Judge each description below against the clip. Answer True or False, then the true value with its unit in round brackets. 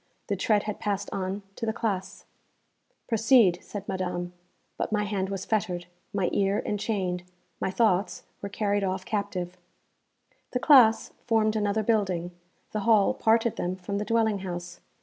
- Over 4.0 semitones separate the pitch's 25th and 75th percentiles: False (2.7 semitones)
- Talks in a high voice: True (200 Hz)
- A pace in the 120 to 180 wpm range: True (150 wpm)